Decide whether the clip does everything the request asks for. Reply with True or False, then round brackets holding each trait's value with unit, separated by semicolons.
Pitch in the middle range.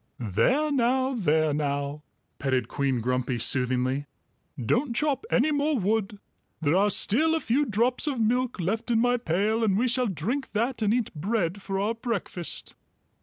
False (215 Hz)